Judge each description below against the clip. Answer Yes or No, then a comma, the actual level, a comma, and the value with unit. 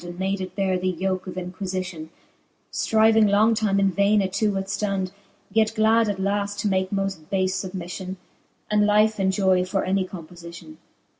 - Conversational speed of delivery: Yes, average, 165 wpm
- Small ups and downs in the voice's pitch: Yes, narrow, 1.9 semitones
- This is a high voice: Yes, high, 195 Hz